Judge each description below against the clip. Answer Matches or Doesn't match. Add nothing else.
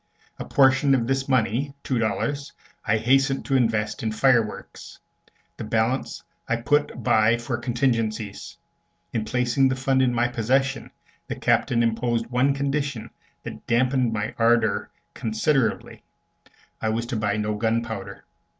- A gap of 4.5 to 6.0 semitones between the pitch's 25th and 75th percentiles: Doesn't match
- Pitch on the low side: Matches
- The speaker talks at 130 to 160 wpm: Matches